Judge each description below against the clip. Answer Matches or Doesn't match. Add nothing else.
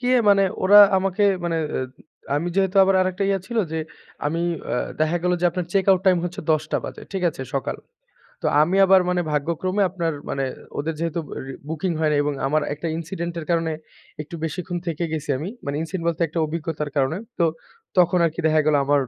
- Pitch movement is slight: Doesn't match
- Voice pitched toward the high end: Doesn't match